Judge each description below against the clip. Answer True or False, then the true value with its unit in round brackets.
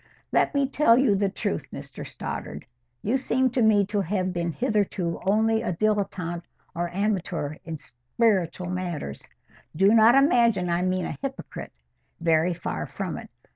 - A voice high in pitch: True (195 Hz)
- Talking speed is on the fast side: False (155 wpm)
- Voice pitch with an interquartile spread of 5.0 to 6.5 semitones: False (4.6 semitones)